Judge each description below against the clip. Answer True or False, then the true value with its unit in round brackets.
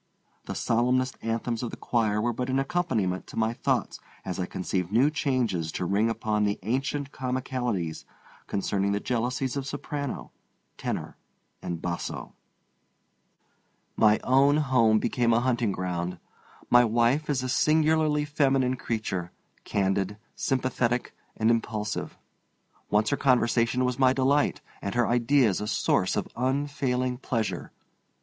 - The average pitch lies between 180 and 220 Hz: False (120 Hz)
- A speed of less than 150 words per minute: True (135 wpm)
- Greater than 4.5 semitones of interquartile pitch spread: False (3.9 semitones)